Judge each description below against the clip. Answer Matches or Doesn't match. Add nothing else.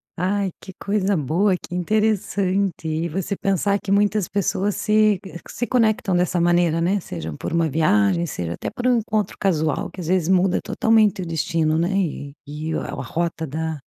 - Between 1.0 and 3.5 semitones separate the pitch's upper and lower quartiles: Doesn't match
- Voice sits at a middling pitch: Matches